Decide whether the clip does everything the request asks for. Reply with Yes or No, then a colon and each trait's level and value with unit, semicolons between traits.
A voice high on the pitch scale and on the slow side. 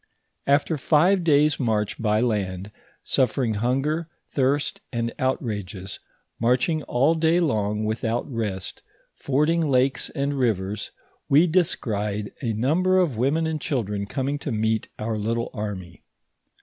No: low, 125 Hz; slow, 125 wpm